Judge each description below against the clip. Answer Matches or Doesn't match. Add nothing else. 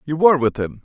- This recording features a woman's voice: Doesn't match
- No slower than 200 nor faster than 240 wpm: Doesn't match